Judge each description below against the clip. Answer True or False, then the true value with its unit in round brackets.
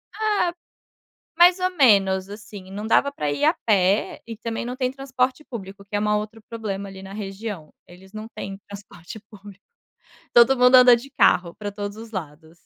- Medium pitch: False (210 Hz)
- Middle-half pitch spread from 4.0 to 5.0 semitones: True (4.3 semitones)